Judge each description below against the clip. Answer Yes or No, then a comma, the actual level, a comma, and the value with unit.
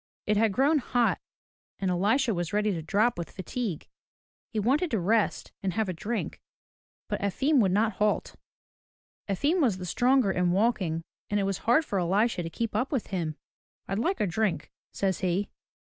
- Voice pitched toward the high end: Yes, high, 205 Hz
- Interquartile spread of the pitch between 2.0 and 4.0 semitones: No, average, 4.5 semitones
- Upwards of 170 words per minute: Yes, average, 180 wpm